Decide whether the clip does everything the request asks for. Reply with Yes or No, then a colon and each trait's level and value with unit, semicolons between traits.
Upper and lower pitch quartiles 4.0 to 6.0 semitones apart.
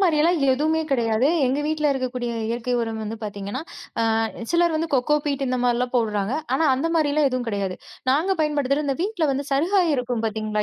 Yes: average, 4.6 semitones